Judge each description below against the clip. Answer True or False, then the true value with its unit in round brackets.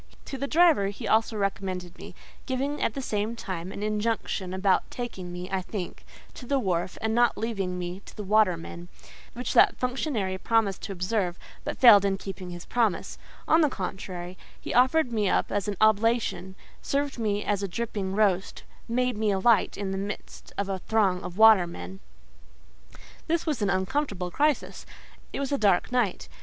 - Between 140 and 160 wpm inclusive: False (175 wpm)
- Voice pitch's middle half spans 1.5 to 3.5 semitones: False (4.1 semitones)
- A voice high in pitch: True (205 Hz)